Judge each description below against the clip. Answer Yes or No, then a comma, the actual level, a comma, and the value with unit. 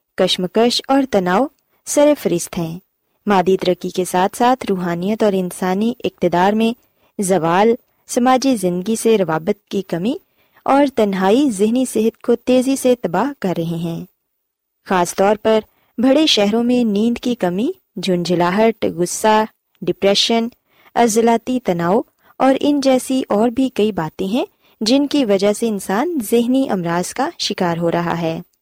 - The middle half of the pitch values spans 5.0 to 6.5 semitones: Yes, average, 5.3 semitones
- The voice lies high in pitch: Yes, high, 215 Hz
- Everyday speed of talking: Yes, average, 145 wpm